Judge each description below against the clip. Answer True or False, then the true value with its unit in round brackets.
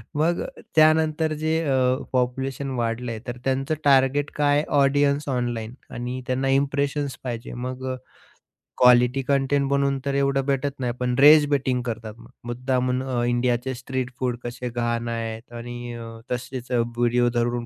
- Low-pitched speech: True (130 Hz)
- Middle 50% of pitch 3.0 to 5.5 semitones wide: False (2.4 semitones)